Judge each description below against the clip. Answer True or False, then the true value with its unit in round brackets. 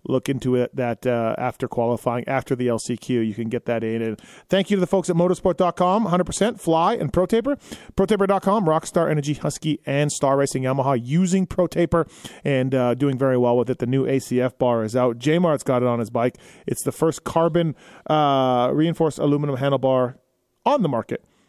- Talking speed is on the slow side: False (190 wpm)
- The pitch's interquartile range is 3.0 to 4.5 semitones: False (5.3 semitones)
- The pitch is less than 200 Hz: True (140 Hz)